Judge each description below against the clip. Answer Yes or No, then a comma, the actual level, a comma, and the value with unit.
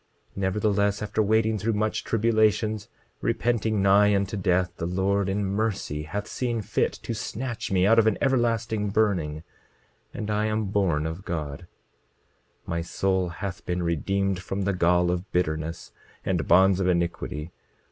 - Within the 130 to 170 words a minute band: Yes, average, 155 wpm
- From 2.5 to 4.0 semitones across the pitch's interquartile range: Yes, average, 3.3 semitones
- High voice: No, low, 100 Hz